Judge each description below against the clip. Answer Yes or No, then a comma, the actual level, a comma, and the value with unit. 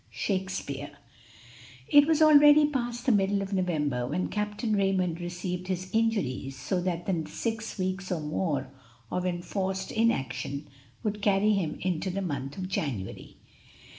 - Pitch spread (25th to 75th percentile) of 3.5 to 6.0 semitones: Yes, average, 4.5 semitones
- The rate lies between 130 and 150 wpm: Yes, average, 140 wpm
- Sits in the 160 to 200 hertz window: Yes, medium, 185 Hz